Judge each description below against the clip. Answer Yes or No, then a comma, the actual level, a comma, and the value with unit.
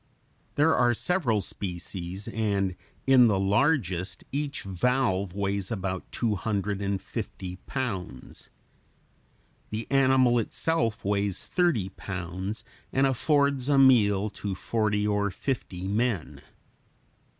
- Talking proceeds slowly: Yes, slow, 110 wpm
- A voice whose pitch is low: Yes, low, 105 Hz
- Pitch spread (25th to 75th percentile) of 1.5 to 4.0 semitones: No, average, 4.9 semitones